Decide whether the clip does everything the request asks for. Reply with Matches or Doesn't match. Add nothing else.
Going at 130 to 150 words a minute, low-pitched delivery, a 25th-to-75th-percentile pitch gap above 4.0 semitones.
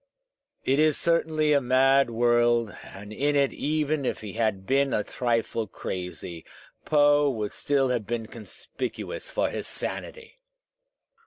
Matches